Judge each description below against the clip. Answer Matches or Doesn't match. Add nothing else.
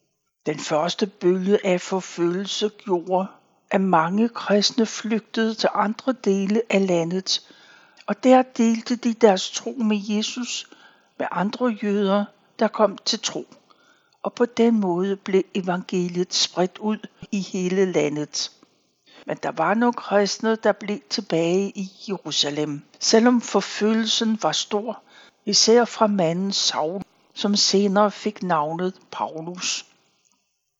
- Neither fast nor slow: Doesn't match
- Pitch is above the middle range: Matches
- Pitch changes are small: Doesn't match